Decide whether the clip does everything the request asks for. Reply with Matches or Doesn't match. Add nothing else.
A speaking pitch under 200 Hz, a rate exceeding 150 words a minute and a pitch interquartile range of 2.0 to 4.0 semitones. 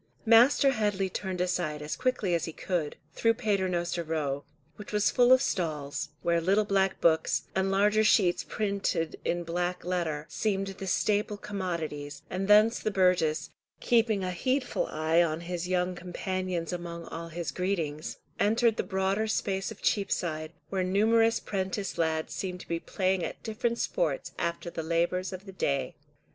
Matches